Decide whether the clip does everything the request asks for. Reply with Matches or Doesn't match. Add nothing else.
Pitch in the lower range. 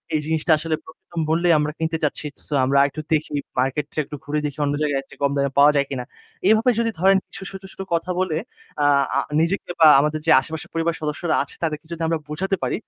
Doesn't match